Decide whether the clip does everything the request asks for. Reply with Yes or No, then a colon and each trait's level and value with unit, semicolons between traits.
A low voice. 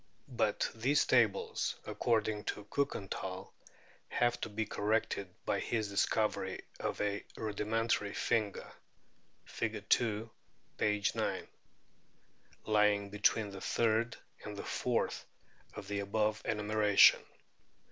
Yes: low, 105 Hz